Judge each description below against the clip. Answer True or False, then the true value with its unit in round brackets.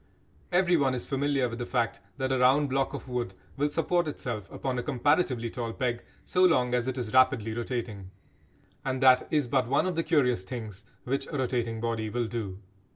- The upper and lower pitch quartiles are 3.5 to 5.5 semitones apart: False (3.1 semitones)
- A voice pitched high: False (125 Hz)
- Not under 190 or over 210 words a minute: True (195 wpm)